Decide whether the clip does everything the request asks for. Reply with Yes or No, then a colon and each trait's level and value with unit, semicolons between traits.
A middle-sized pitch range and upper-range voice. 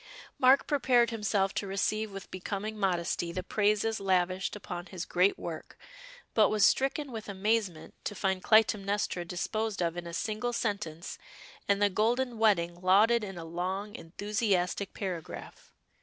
Yes: average, 3.1 semitones; high, 200 Hz